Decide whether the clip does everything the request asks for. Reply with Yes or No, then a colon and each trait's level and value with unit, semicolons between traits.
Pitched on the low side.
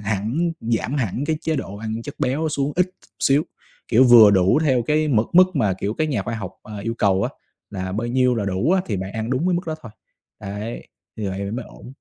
Yes: low, 115 Hz